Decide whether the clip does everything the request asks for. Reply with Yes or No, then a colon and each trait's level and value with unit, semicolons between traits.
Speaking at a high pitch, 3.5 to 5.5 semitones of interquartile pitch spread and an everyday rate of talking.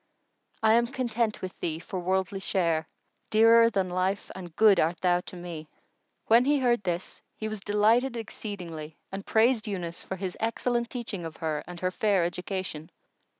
Yes: high, 195 Hz; average, 4.2 semitones; average, 175 wpm